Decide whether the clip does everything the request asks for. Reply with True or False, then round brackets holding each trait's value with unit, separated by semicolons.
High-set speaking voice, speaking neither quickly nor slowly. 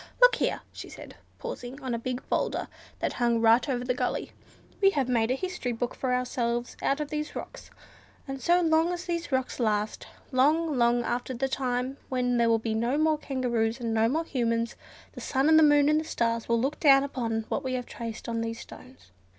False (255 Hz; 215 wpm)